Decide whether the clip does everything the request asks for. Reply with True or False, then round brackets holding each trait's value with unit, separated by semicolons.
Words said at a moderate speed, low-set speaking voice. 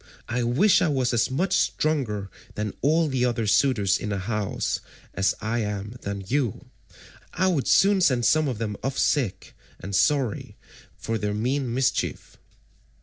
True (160 wpm; 120 Hz)